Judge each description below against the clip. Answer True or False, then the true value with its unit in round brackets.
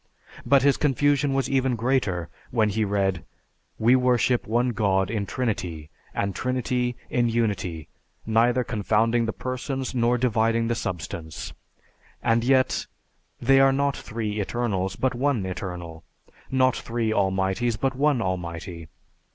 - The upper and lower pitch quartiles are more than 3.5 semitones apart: True (4.9 semitones)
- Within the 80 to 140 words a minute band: True (135 wpm)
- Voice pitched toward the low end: True (115 Hz)